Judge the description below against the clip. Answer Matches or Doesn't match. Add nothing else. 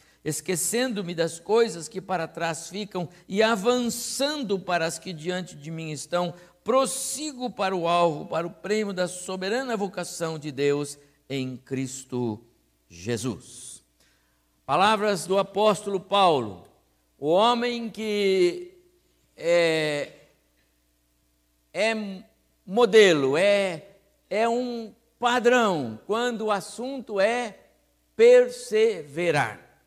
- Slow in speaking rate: Matches